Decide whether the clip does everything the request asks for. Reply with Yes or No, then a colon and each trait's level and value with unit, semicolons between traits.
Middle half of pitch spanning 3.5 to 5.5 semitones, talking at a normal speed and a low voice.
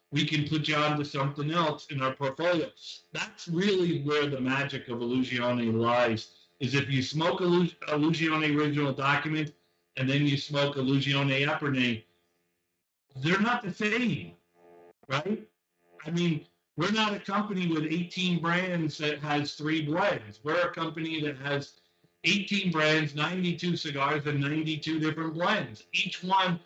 No: average, 4.2 semitones; average, 150 wpm; medium, 150 Hz